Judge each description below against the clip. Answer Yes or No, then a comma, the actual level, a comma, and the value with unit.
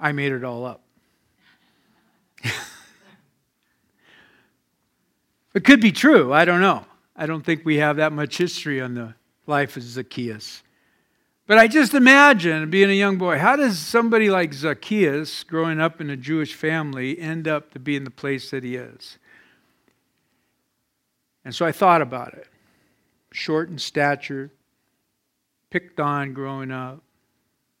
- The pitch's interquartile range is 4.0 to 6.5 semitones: Yes, average, 4.6 semitones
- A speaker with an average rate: Yes, average, 145 wpm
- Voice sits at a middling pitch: Yes, medium, 155 Hz